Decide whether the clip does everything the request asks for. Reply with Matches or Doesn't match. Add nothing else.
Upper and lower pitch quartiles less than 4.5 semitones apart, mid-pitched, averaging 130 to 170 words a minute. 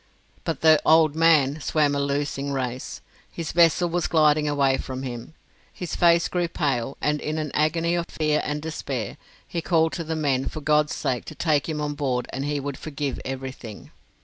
Doesn't match